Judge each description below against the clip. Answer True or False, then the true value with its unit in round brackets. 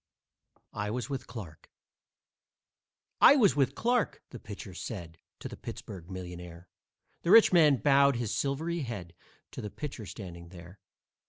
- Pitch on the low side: True (110 Hz)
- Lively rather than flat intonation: True (7.8 semitones)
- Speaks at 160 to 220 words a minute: False (145 wpm)